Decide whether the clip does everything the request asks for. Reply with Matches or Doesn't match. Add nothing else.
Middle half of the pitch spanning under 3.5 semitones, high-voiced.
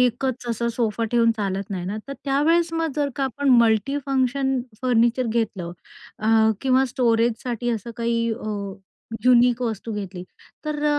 Matches